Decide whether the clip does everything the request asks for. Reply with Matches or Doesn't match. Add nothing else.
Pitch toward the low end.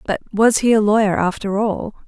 Doesn't match